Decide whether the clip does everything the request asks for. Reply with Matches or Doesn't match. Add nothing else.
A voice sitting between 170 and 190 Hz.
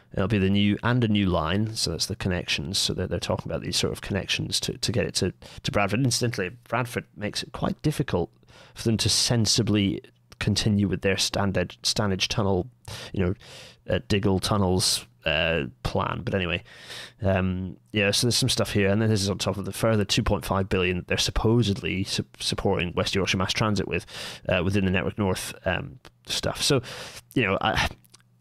Doesn't match